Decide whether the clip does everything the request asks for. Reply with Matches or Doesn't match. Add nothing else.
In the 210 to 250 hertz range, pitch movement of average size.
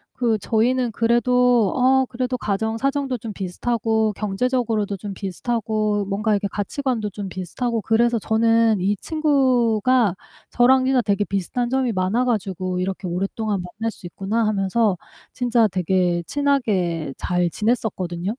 Matches